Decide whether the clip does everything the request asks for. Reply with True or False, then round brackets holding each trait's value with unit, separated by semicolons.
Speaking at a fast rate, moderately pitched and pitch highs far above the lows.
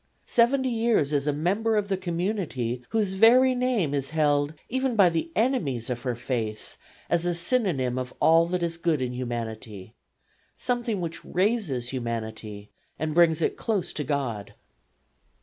False (150 wpm; 165 Hz; 8.6 semitones)